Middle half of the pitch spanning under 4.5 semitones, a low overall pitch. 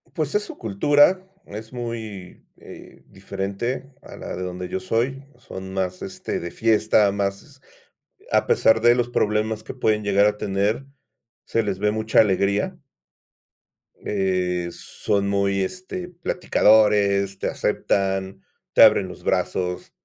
Yes: average, 2.8 semitones; low, 105 Hz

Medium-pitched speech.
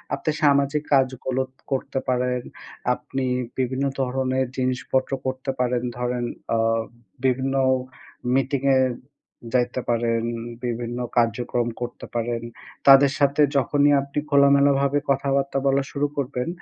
No: low, 130 Hz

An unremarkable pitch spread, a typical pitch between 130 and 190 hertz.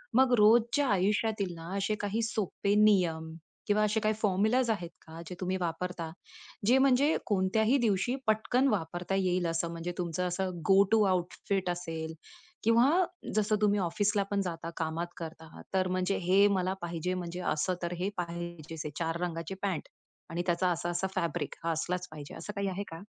Yes: average, 3.6 semitones; medium, 185 Hz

